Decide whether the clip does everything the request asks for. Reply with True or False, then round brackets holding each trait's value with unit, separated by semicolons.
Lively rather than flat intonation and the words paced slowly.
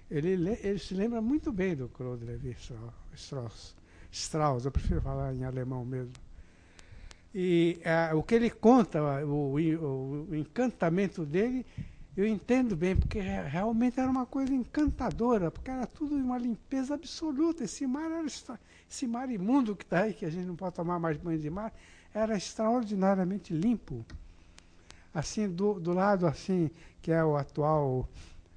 False (9.0 semitones; 155 wpm)